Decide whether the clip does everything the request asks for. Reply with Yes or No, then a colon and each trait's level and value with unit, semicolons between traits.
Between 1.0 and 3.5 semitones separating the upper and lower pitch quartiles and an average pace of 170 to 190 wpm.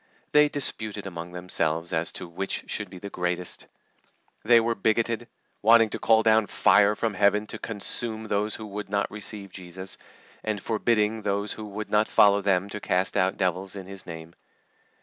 Yes: average, 2.7 semitones; average, 175 wpm